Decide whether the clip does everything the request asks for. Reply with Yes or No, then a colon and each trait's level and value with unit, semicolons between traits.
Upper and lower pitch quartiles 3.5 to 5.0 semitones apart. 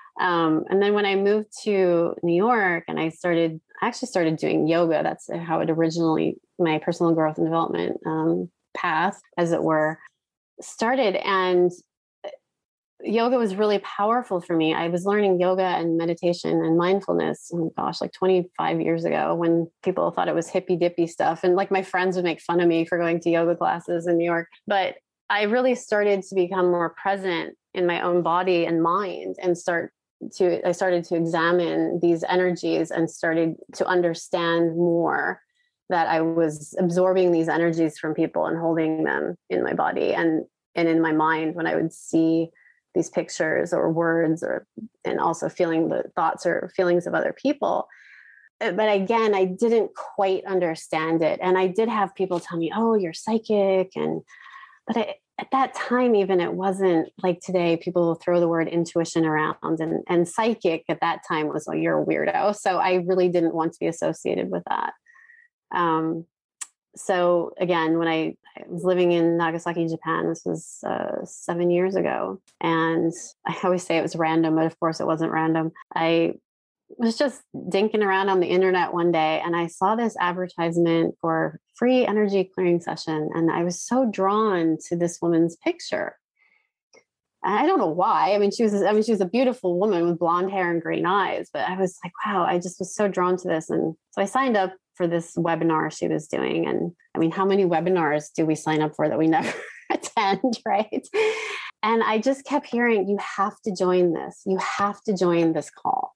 No: average, 3.0 semitones